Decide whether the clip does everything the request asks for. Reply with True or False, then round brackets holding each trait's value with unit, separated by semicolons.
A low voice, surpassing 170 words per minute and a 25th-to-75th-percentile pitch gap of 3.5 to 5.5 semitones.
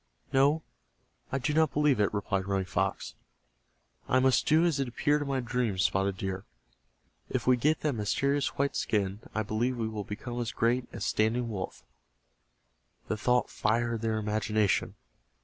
False (120 Hz; 165 wpm; 4.3 semitones)